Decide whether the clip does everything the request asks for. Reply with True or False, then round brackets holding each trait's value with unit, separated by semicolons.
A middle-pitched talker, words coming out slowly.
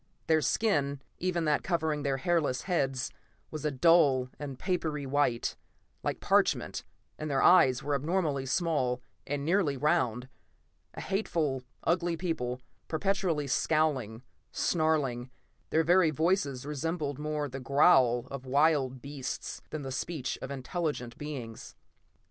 True (145 Hz; 130 wpm)